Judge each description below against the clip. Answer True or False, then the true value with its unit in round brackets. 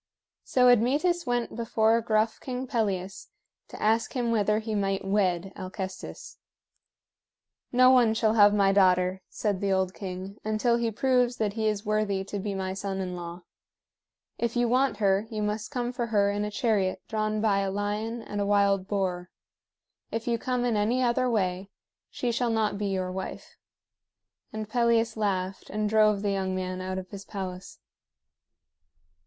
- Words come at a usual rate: True (170 wpm)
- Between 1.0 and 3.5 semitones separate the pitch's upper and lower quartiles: True (3.1 semitones)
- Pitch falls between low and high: False (210 Hz)